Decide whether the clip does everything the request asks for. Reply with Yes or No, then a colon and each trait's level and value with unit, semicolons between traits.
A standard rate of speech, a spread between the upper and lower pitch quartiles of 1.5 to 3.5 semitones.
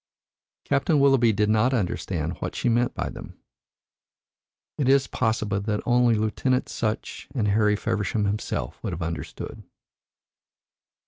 No: slow, 130 wpm; average, 3.1 semitones